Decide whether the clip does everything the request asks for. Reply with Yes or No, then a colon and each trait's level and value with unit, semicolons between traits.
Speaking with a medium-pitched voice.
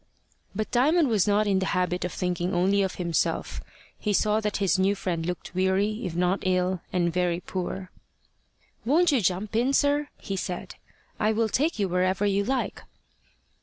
No: high, 195 Hz